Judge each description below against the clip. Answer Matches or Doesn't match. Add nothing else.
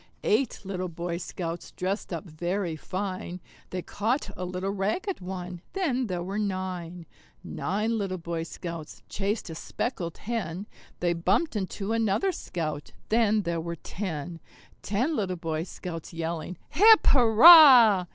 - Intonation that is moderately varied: Matches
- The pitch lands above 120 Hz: Matches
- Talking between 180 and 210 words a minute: Doesn't match